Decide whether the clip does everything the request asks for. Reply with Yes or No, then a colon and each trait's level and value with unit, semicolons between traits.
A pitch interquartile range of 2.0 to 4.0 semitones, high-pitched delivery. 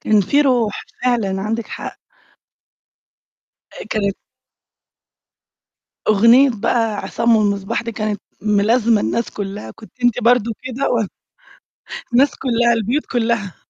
Yes: narrow, 2.5 semitones; high, 230 Hz